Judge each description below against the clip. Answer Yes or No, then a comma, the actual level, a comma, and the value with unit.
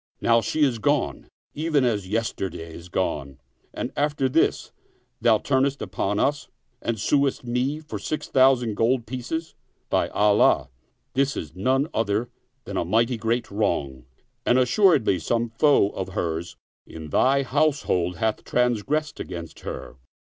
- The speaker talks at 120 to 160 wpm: Yes, average, 150 wpm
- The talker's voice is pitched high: No, low, 115 Hz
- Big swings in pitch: Yes, wide, 5.8 semitones